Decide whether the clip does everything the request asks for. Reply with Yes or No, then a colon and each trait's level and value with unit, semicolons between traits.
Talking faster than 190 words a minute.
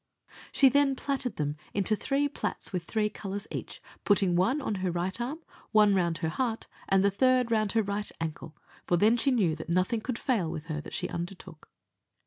Yes: fast, 205 wpm